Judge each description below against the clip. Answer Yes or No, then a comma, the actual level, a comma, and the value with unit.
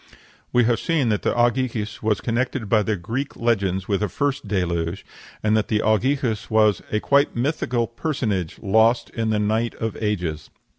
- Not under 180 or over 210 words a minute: No, average, 160 wpm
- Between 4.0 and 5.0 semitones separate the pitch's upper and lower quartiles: No, average, 2.7 semitones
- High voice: No, low, 110 Hz